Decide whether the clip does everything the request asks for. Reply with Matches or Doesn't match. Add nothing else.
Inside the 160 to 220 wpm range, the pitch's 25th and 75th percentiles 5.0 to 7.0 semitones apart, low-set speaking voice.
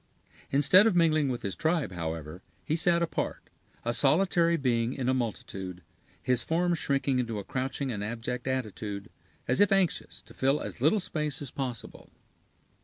Matches